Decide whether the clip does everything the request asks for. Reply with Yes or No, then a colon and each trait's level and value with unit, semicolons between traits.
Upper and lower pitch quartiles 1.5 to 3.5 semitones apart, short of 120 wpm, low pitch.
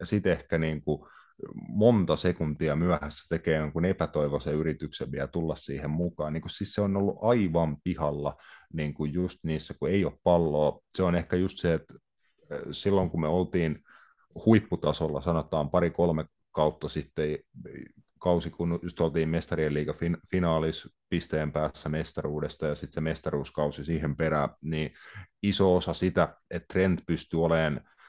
No: narrow, 2.6 semitones; average, 145 wpm; very low, 80 Hz